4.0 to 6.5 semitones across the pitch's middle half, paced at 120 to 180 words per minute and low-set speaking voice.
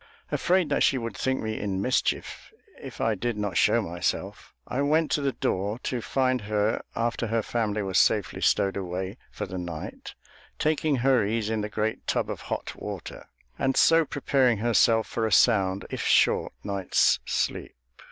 Yes: average, 4.3 semitones; average, 175 wpm; low, 110 Hz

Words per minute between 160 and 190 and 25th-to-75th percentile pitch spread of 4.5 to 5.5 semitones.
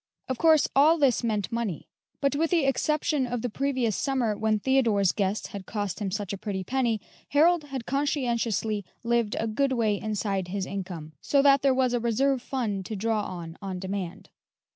Yes: average, 185 wpm; average, 5.1 semitones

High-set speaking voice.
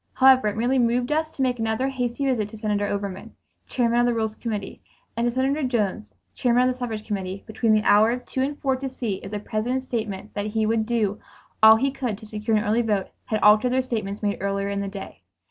Yes: high, 225 Hz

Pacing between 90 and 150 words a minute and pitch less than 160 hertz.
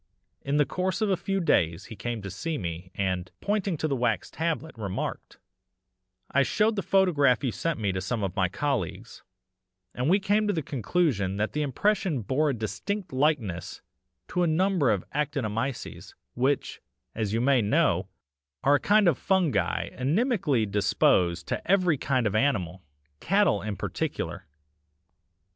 No: average, 160 wpm; low, 135 Hz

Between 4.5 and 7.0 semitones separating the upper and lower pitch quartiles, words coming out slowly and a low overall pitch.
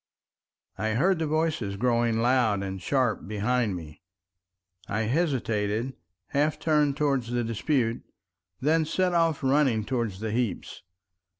Yes: wide, 5.4 semitones; slow, 125 wpm; low, 120 Hz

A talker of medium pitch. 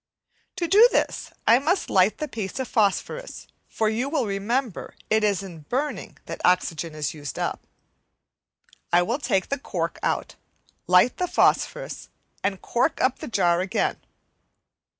No: high, 215 Hz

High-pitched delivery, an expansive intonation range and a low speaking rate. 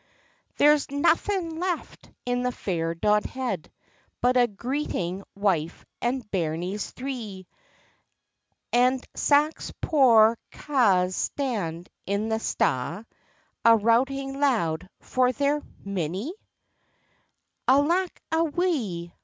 Yes: high, 240 Hz; wide, 6.8 semitones; slow, 95 wpm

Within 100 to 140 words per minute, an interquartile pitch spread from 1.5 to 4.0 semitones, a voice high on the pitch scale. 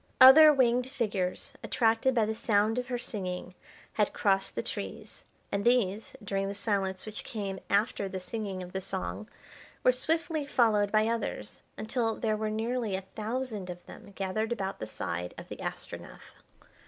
No: average, 165 wpm; average, 3.7 semitones; high, 215 Hz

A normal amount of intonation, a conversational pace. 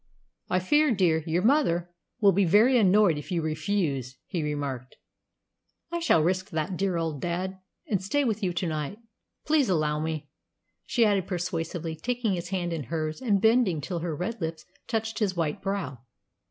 Yes: average, 4.4 semitones; average, 175 wpm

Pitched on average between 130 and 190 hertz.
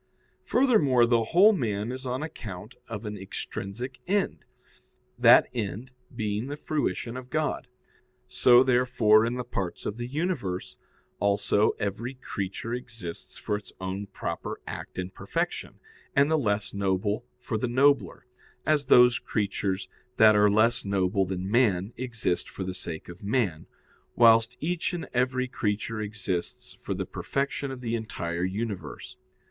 No: low, 115 Hz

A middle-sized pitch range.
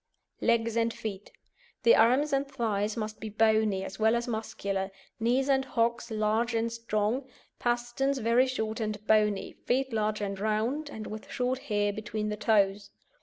No: narrow, 2.3 semitones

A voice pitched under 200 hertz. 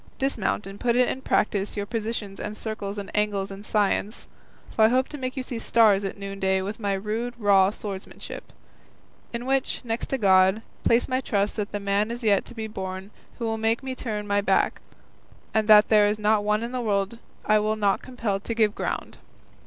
No: high, 210 Hz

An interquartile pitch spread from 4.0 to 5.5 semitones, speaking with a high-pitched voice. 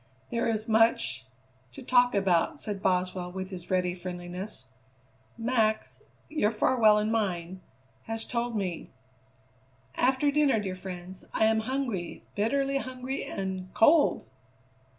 Yes: average, 4.6 semitones; high, 210 Hz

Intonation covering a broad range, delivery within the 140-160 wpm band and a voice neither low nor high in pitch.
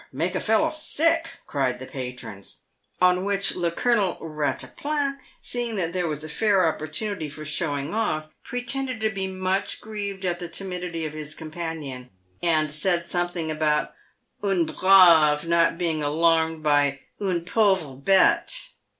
No: average, 4.2 semitones; average, 150 wpm; medium, 170 Hz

